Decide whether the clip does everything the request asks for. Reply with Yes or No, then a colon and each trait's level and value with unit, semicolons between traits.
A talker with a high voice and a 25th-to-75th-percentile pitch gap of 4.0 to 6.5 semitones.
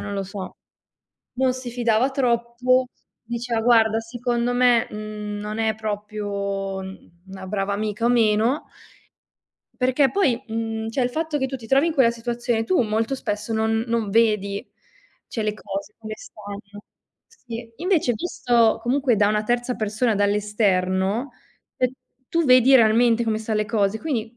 No: high, 225 Hz; average, 2.7 semitones